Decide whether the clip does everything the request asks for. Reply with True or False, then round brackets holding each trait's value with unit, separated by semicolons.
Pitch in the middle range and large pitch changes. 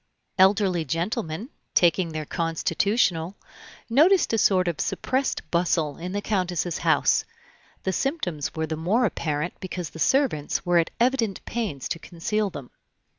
False (180 Hz; 4.7 semitones)